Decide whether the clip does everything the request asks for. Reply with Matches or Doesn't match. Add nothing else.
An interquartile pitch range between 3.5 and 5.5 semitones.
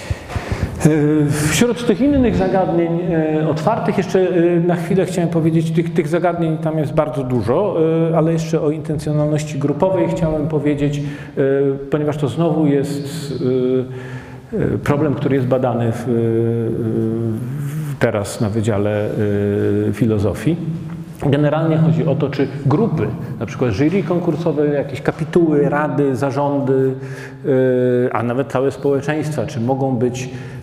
Matches